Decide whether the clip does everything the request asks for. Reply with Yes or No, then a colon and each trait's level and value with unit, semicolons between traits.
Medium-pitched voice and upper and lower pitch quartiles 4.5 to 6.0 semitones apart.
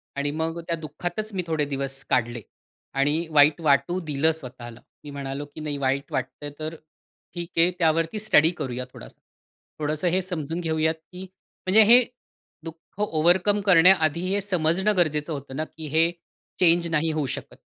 No: medium, 160 Hz; average, 3.3 semitones